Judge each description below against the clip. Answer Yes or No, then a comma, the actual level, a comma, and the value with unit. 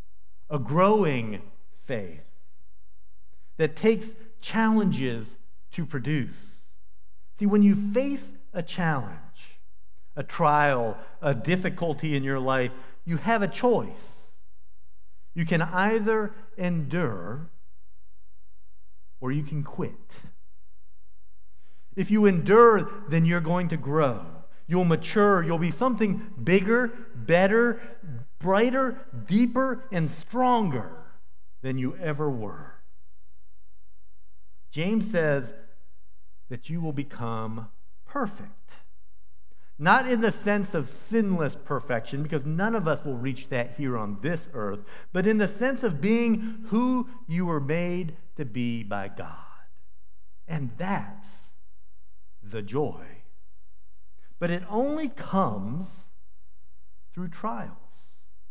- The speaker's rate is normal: No, slow, 110 wpm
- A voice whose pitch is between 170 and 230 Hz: No, medium, 145 Hz